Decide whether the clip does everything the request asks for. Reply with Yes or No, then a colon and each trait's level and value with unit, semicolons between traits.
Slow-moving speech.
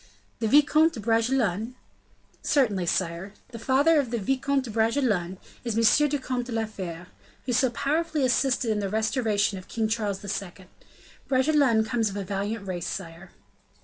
No: average, 165 wpm